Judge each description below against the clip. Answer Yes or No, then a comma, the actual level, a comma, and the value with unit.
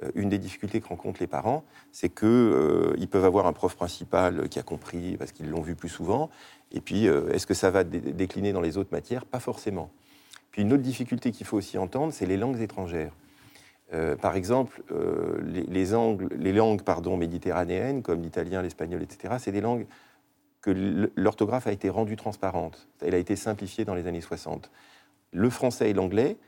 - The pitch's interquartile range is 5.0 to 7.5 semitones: No, average, 3.9 semitones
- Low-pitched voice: Yes, low, 100 Hz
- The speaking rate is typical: Yes, average, 195 wpm